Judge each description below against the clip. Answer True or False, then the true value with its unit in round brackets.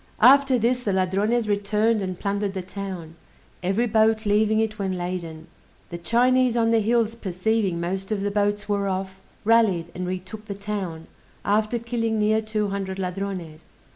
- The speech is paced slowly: False (165 wpm)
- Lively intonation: False (2.8 semitones)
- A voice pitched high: True (205 Hz)